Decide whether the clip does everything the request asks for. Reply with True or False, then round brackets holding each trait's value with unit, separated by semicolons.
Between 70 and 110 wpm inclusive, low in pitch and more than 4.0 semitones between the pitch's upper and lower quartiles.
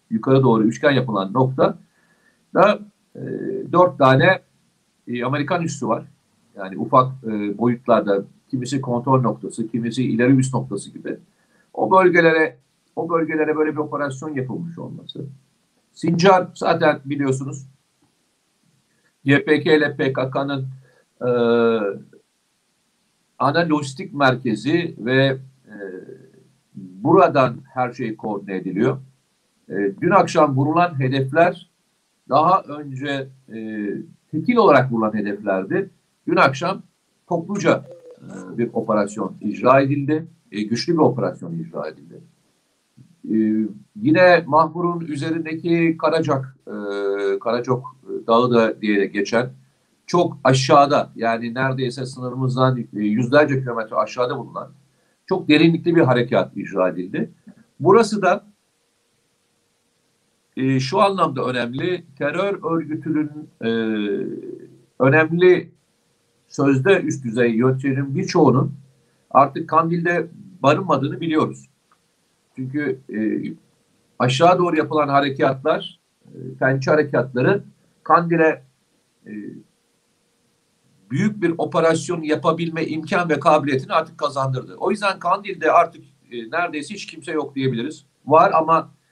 False (105 wpm; 145 Hz; 5.2 semitones)